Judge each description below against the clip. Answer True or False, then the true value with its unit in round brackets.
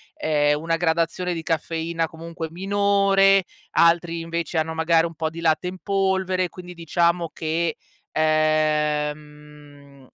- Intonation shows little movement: True (2.2 semitones)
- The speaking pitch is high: False (165 Hz)